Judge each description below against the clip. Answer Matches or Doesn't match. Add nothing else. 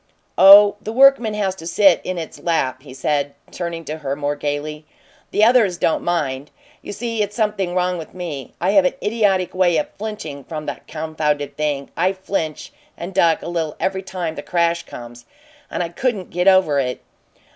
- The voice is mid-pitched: Matches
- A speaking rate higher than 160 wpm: Matches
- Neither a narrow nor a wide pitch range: Matches